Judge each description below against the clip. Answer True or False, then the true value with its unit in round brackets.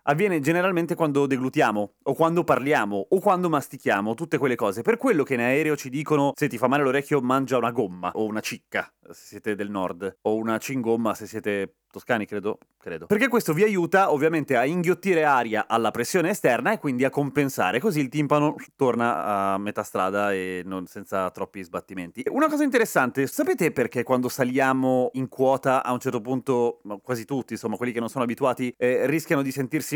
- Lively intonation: True (5.7 semitones)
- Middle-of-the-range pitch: False (130 Hz)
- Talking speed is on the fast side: True (190 wpm)